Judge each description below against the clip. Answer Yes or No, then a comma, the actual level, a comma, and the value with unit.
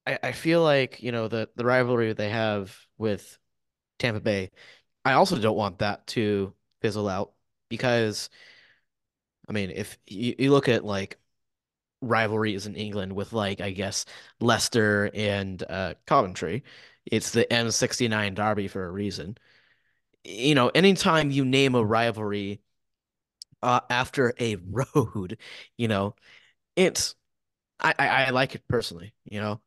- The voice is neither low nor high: No, low, 110 Hz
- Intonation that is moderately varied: Yes, average, 3.1 semitones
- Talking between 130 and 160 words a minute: Yes, average, 150 wpm